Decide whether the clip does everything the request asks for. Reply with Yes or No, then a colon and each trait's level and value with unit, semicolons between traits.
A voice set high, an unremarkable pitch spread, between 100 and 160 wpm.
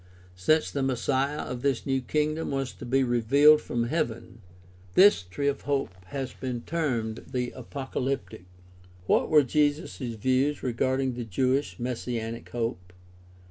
No: low, 130 Hz; average, 3.0 semitones; average, 140 wpm